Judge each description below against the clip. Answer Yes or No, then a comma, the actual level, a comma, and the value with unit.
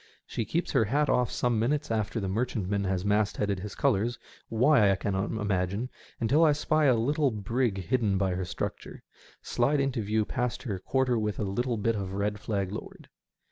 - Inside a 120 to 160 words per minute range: No, average, 190 wpm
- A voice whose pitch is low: Yes, low, 110 Hz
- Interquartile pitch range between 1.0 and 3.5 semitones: No, average, 4.0 semitones